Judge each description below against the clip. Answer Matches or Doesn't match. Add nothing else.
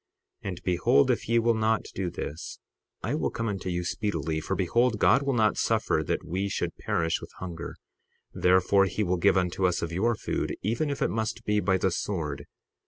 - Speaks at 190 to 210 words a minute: Matches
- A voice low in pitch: Matches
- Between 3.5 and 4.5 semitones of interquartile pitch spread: Matches